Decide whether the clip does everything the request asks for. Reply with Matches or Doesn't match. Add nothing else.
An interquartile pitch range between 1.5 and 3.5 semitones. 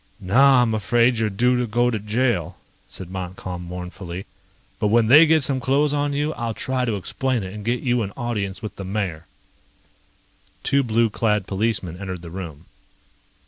Doesn't match